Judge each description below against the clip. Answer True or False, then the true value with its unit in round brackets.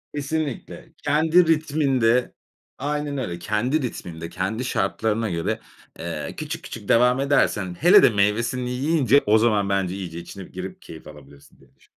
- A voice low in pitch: True (115 Hz)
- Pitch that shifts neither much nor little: False (7.0 semitones)